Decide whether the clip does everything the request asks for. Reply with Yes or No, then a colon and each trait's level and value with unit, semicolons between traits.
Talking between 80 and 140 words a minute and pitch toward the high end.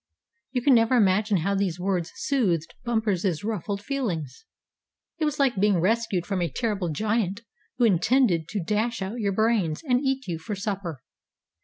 No: average, 165 wpm; high, 205 Hz